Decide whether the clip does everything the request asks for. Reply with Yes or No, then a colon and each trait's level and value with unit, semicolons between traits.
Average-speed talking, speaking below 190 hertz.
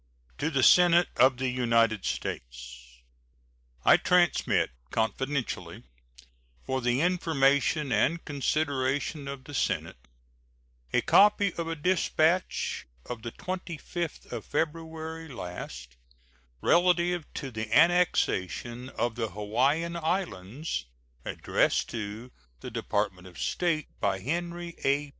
No: slow, 110 wpm; medium, 140 Hz